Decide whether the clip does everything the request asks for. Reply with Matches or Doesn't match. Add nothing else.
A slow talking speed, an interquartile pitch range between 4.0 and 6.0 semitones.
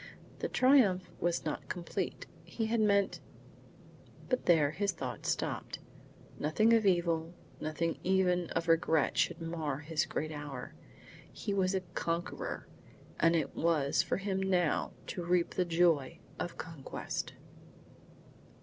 Doesn't match